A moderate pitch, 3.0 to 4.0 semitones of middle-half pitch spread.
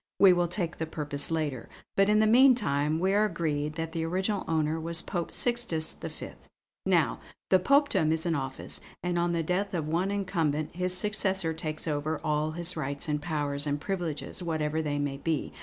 Yes: medium, 165 Hz; average, 3.5 semitones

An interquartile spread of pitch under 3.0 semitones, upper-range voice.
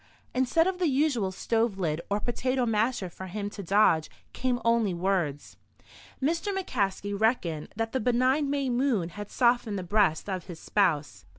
No: average, 5.2 semitones; high, 215 Hz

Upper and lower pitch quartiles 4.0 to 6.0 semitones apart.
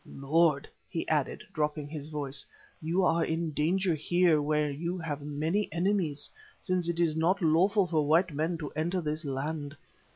No: narrow, 2.5 semitones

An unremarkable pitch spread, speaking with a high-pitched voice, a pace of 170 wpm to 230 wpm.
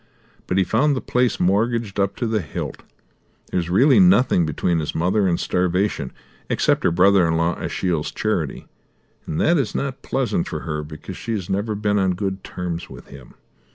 No: average, 4.5 semitones; very low, 95 Hz; average, 190 wpm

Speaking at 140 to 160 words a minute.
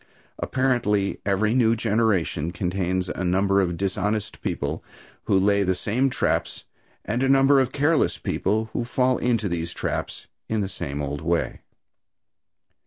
Yes: average, 145 wpm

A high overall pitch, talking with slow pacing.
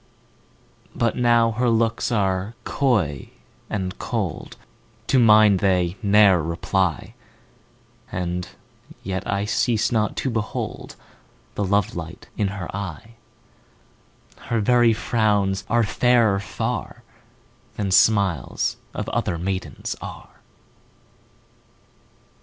No: low, 100 Hz; slow, 105 wpm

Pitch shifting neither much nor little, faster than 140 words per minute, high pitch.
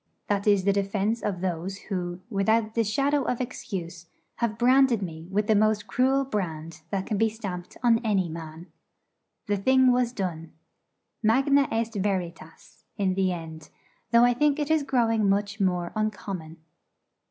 Yes: average, 4.3 semitones; average, 160 wpm; high, 205 Hz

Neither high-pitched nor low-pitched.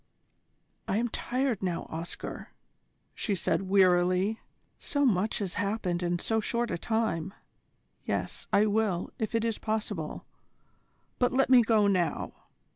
No: high, 205 Hz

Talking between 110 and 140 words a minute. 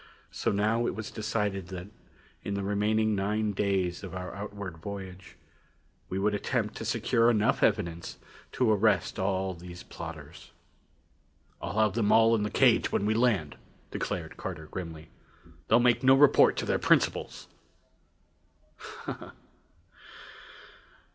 Yes: slow, 135 wpm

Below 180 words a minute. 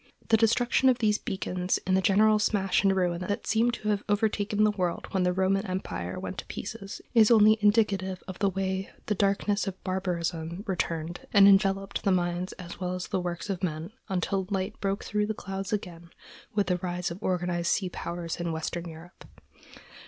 No: average, 190 wpm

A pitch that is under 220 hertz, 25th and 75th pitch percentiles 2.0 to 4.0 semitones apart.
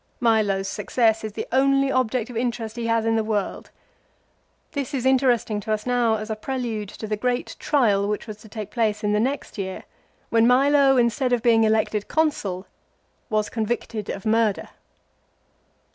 No: high, 225 Hz; average, 2.7 semitones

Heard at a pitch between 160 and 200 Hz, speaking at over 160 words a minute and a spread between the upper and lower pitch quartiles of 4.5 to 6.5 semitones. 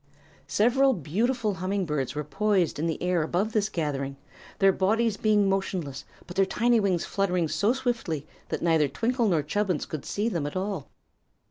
Yes: high, 190 Hz; average, 170 wpm; average, 5.1 semitones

